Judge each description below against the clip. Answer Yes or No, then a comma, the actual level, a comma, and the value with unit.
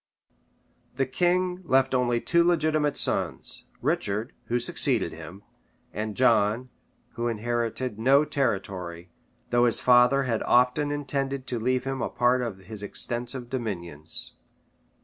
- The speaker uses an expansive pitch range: No, average, 3.6 semitones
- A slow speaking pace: Yes, slow, 130 wpm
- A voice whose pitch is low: Yes, low, 125 Hz